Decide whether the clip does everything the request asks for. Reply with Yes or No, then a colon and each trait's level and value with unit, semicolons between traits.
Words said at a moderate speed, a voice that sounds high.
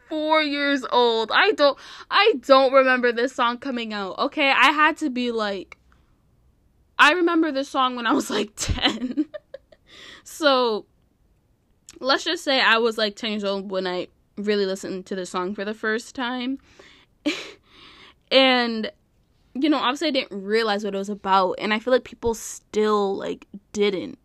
Yes: average, 165 wpm; high, 245 Hz